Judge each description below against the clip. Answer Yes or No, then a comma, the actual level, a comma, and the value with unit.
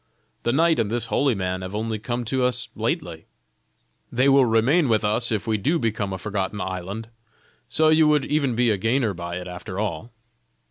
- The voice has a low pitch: Yes, low, 115 Hz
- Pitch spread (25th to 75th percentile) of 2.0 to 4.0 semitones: No, average, 4.6 semitones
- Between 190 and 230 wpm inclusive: Yes, average, 195 wpm